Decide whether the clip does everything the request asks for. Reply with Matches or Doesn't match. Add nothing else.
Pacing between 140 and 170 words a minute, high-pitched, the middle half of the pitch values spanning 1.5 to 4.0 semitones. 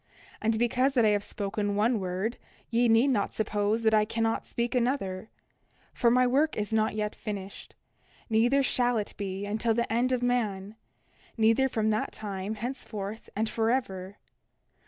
Matches